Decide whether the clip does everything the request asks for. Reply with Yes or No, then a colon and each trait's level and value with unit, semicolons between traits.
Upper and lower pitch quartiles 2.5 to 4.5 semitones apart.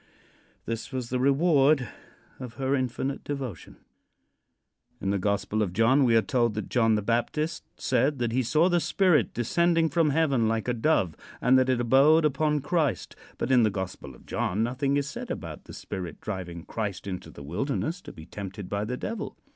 No: average, 5.2 semitones